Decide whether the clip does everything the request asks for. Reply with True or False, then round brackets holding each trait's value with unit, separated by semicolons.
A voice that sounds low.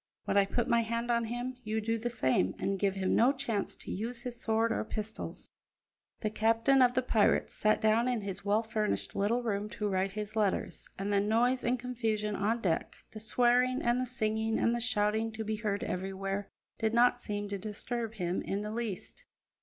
False (220 Hz)